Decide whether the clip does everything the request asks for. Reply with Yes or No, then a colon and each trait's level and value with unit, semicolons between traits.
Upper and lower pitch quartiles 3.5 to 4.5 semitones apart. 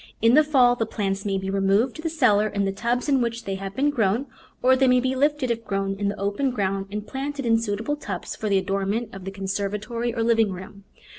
Yes: average, 4.2 semitones